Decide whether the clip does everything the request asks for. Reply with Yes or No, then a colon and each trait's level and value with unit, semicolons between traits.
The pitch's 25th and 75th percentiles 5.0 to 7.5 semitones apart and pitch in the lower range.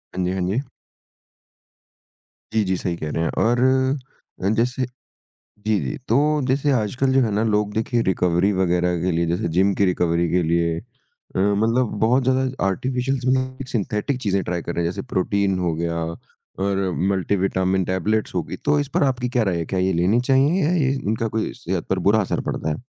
Yes: average, 5.3 semitones; low, 100 Hz